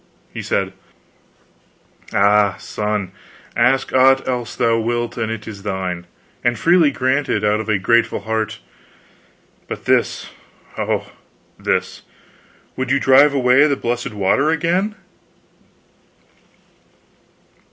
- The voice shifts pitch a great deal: No, average, 4.1 semitones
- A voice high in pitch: No, low, 120 Hz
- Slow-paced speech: Yes, slow, 110 wpm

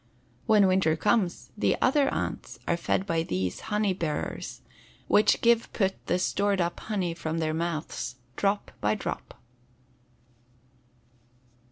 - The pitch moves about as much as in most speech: Yes, average, 4.2 semitones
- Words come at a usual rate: No, slow, 130 wpm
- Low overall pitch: No, medium, 185 Hz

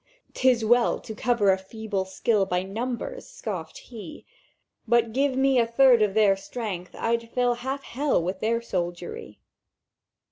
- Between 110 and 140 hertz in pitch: No, high, 230 Hz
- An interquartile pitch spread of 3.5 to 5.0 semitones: Yes, average, 4.4 semitones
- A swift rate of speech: No, average, 150 wpm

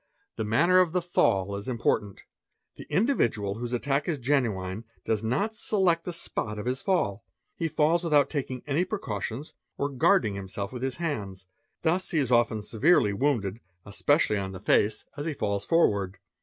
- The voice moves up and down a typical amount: No, wide, 7.8 semitones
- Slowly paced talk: No, average, 170 wpm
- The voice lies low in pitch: Yes, low, 125 Hz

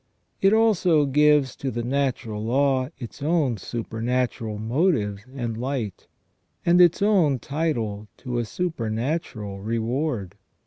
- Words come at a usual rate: No, slow, 120 wpm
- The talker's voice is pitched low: Yes, low, 130 Hz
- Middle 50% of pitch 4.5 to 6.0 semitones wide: Yes, average, 5.2 semitones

